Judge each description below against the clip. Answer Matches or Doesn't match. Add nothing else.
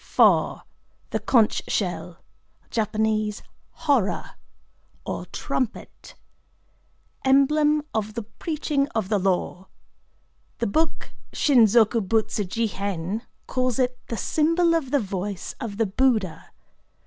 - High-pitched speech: Matches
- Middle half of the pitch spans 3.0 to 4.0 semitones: Doesn't match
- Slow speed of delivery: Matches